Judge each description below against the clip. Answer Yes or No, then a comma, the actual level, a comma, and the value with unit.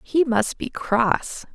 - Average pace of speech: Yes, average, 155 wpm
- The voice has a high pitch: Yes, high, 245 Hz